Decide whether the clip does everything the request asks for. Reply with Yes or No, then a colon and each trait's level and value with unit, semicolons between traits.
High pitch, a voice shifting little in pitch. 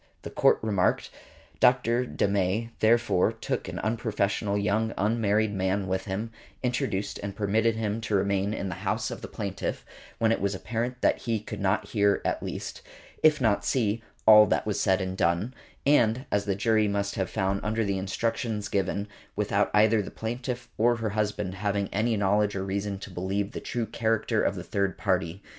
No: low, 105 Hz; narrow, 2.3 semitones